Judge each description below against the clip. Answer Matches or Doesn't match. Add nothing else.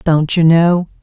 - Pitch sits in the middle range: Matches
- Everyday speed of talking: Matches